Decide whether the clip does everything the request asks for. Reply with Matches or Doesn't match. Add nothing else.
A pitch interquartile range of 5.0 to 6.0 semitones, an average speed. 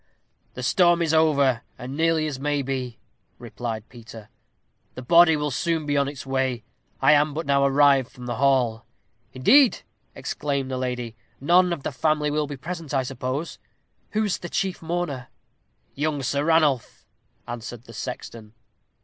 Doesn't match